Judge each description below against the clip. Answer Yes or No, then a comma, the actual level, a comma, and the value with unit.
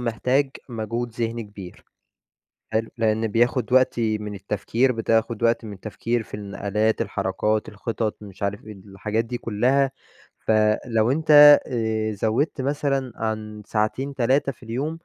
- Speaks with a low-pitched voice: Yes, low, 115 Hz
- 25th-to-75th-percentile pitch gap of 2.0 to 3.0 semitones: Yes, average, 2.7 semitones